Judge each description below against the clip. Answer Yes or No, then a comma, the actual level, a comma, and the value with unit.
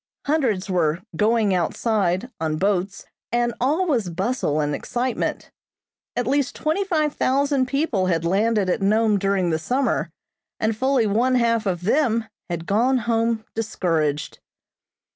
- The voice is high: Yes, high, 220 Hz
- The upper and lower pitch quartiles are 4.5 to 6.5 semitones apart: Yes, wide, 5.6 semitones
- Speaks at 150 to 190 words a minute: No, average, 140 wpm